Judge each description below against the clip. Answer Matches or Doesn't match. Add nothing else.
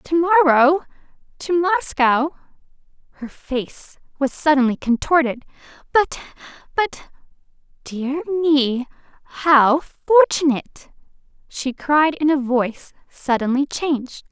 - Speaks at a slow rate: Matches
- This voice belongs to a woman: Matches